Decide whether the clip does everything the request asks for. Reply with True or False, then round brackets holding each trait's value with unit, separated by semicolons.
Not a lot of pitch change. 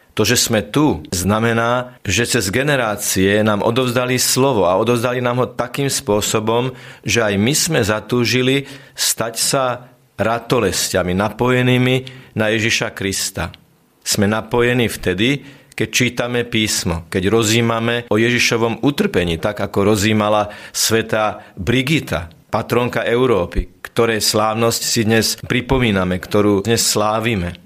False (3.0 semitones)